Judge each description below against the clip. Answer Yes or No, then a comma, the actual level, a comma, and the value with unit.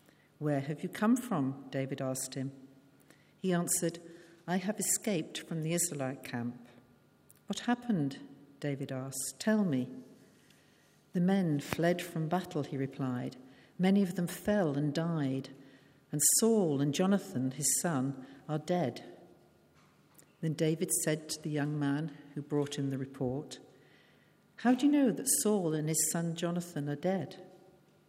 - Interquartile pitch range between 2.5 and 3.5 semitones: No, average, 4.7 semitones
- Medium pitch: Yes, medium, 155 Hz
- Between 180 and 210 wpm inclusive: No, average, 145 wpm